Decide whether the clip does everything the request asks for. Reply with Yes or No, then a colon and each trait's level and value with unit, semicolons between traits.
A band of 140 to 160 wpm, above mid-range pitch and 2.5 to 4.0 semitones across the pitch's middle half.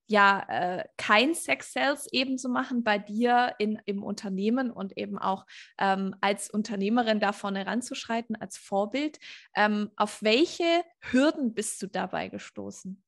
Yes: average, 145 wpm; high, 210 Hz; average, 3.7 semitones